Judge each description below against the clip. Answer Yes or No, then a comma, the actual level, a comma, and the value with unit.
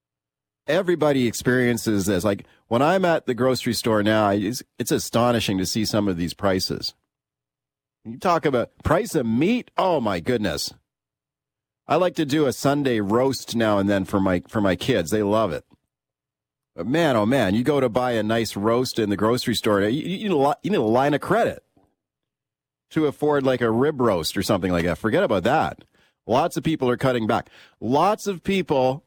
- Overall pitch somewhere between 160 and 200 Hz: No, low, 120 Hz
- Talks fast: No, average, 195 wpm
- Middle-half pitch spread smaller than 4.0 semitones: No, average, 4.8 semitones